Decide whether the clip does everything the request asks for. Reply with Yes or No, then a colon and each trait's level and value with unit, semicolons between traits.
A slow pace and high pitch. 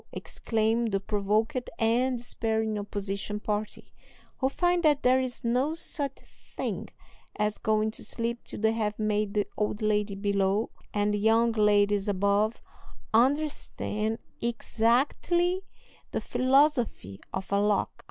Yes: slow, 130 wpm; high, 220 Hz